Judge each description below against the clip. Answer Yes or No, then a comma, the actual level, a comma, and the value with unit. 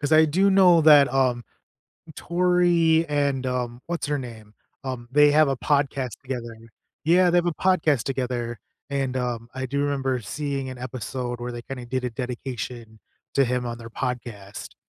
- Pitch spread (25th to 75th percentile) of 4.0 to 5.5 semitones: No, average, 3.4 semitones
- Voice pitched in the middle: No, low, 130 Hz